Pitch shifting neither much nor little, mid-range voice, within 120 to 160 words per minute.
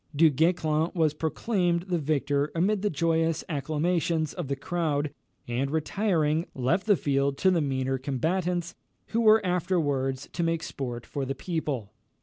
Yes: average, 3.9 semitones; medium, 160 Hz; average, 150 wpm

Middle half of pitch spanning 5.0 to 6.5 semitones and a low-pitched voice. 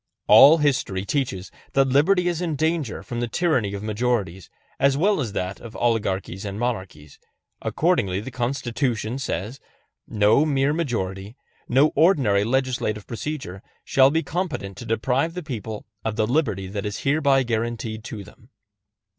Yes: wide, 5.5 semitones; low, 120 Hz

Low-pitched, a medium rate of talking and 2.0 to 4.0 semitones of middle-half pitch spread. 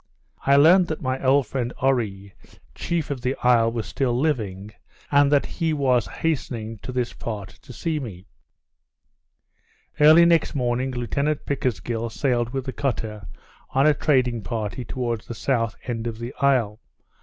Yes: low, 125 Hz; average, 155 wpm; average, 3.6 semitones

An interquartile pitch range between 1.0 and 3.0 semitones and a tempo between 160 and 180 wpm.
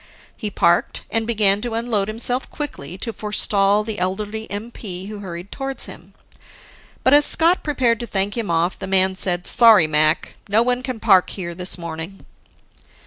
No: average, 3.9 semitones; average, 170 wpm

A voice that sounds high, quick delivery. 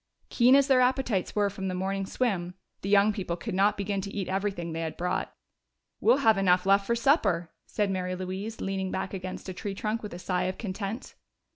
Yes: high, 195 Hz; fast, 215 wpm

